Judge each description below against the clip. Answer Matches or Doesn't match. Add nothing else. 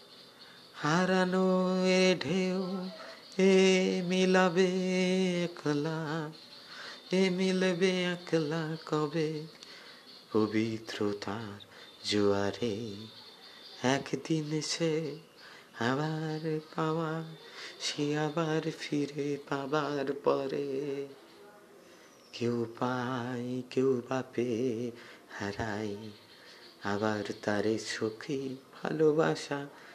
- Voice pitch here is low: Doesn't match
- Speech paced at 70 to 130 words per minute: Doesn't match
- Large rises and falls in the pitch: Matches